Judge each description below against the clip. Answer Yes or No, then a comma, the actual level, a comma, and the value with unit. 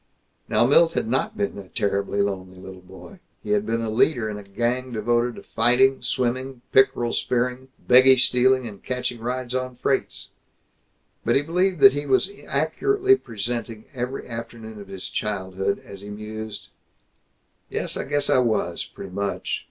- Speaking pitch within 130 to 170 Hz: No, low, 120 Hz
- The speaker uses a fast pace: No, average, 165 wpm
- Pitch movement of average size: Yes, average, 4.1 semitones